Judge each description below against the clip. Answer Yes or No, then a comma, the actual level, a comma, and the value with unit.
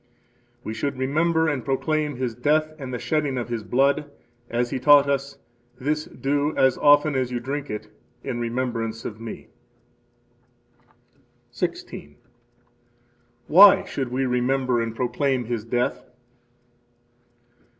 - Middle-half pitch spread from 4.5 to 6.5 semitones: No, average, 3.2 semitones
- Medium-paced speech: No, slow, 130 wpm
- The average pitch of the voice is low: Yes, low, 130 Hz